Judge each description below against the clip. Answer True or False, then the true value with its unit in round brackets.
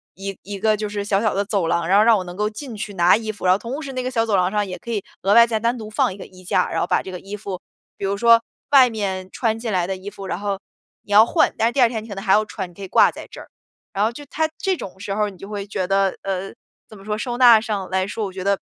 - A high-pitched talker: True (205 Hz)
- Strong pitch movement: False (2.6 semitones)